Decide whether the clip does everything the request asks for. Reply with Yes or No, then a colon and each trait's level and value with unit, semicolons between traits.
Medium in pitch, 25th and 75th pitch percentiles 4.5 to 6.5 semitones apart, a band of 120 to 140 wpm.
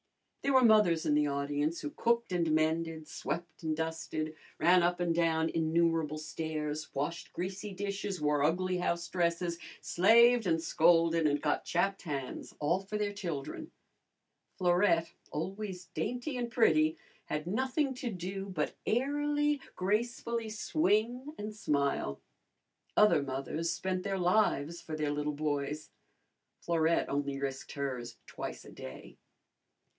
Yes: medium, 170 Hz; average, 4.9 semitones; slow, 135 wpm